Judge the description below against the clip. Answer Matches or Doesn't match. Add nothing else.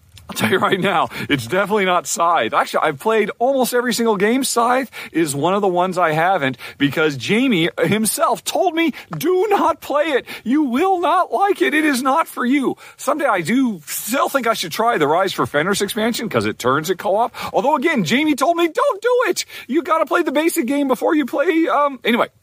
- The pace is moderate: Doesn't match